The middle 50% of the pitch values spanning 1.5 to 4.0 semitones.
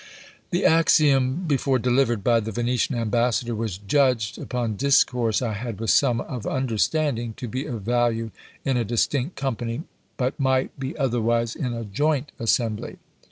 Yes: average, 2.8 semitones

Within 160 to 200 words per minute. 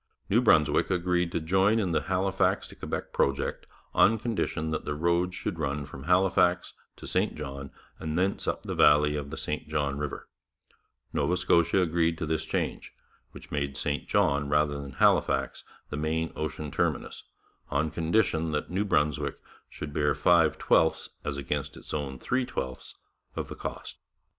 Yes: average, 165 wpm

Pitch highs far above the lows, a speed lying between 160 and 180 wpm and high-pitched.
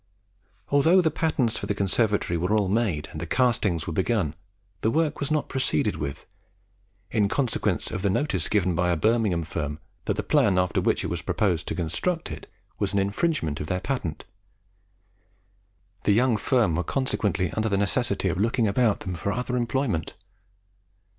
No: wide, 5.9 semitones; average, 175 wpm; low, 100 Hz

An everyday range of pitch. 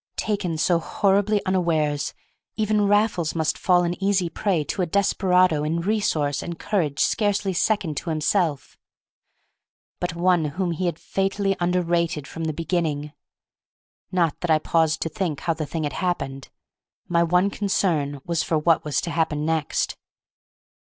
Yes: average, 3.4 semitones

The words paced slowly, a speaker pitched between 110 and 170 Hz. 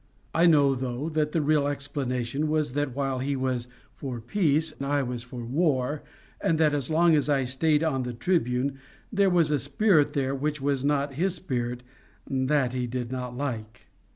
No: average, 180 wpm; medium, 140 Hz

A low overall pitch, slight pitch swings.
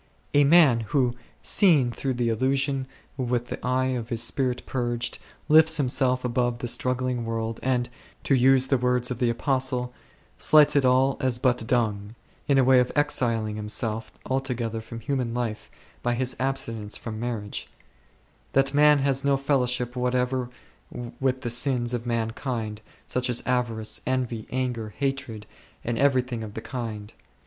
Yes: low, 125 Hz; narrow, 2.2 semitones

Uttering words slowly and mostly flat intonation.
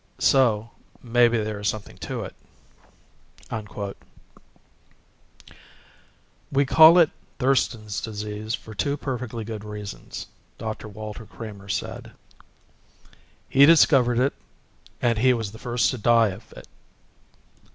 No: slow, 115 wpm; average, 3.1 semitones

